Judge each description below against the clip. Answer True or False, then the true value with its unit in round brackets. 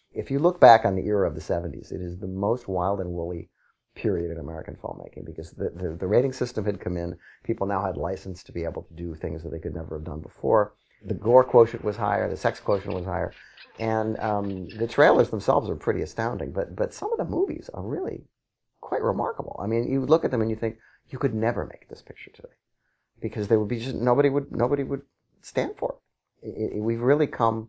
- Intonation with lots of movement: False (4.8 semitones)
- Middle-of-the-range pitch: False (105 Hz)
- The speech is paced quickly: True (235 wpm)